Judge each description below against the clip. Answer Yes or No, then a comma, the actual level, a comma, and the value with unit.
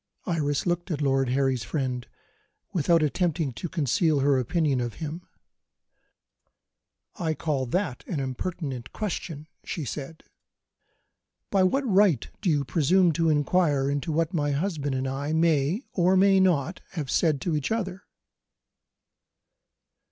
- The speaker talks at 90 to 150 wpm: Yes, slow, 135 wpm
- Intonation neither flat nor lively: Yes, average, 4.2 semitones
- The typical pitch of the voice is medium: Yes, medium, 155 Hz